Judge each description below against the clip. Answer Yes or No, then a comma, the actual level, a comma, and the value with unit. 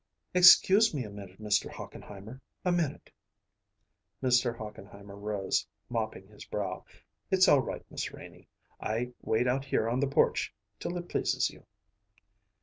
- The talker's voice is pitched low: Yes, low, 115 Hz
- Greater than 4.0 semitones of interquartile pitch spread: Yes, average, 5.1 semitones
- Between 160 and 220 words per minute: No, average, 145 wpm